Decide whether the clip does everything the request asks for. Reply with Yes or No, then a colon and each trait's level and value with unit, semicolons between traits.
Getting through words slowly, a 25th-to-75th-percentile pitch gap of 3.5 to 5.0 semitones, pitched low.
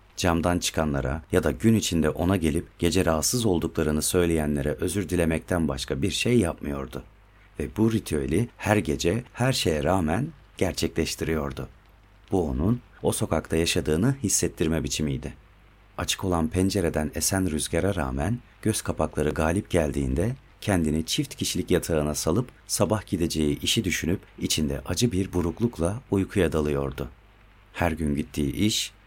No: average, 130 wpm; average, 4.7 semitones; very low, 90 Hz